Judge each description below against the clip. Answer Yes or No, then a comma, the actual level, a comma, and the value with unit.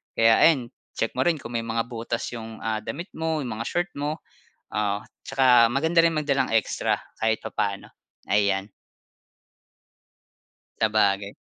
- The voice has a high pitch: No, low, 115 Hz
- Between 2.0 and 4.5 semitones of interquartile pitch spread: No, average, 5.0 semitones